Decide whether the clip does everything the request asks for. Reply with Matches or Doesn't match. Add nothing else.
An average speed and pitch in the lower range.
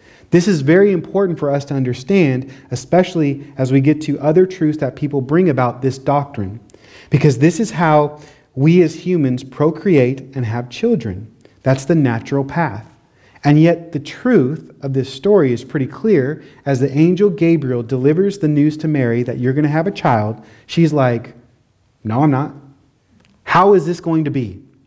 Doesn't match